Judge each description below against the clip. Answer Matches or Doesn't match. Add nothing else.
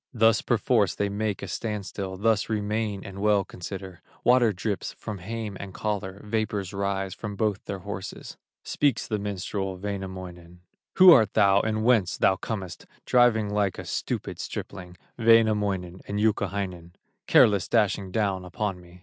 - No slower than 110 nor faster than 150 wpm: Matches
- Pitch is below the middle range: Matches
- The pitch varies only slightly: Matches